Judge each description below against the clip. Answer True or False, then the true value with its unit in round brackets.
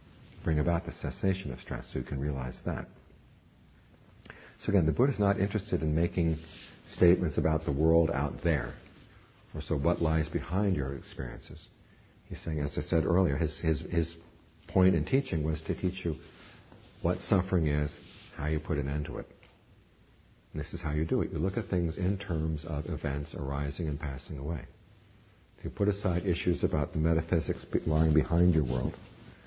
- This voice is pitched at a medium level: False (85 Hz)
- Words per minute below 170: False (185 wpm)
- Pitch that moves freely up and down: False (3.5 semitones)